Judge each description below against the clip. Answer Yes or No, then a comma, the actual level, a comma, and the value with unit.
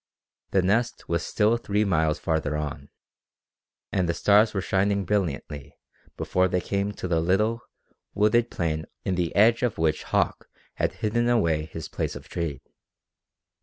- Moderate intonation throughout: Yes, average, 4.6 semitones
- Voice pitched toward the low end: Yes, very low, 95 Hz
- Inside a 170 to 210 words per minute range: No, average, 155 wpm